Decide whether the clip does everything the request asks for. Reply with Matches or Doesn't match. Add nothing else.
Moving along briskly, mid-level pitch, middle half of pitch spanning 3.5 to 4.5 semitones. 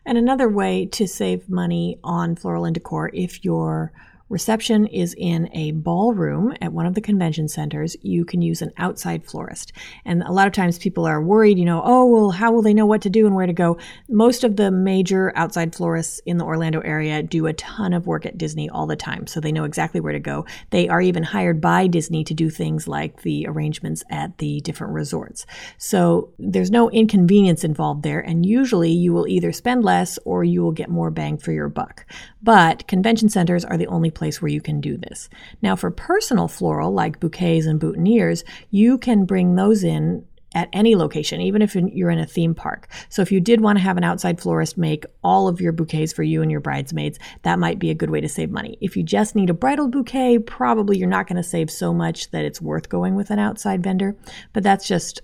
Matches